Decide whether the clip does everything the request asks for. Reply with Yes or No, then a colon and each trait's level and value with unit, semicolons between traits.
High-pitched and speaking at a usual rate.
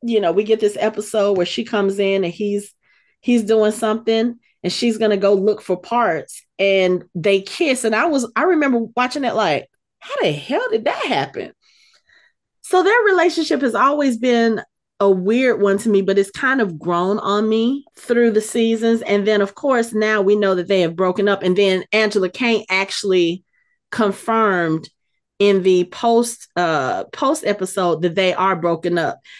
Yes: high, 215 Hz; average, 180 wpm